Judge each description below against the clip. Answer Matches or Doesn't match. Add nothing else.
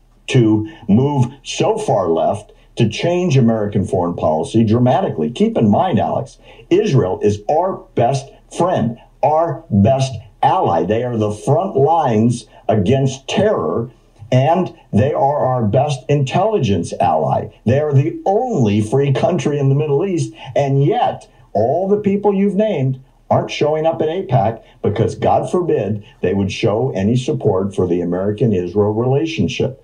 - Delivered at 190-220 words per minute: Doesn't match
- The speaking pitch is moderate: Doesn't match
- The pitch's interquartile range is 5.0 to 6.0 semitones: Matches